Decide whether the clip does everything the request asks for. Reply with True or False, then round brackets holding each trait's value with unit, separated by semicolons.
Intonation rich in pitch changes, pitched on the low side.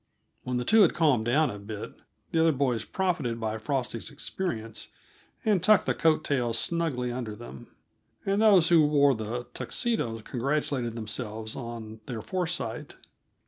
True (6.2 semitones; 125 Hz)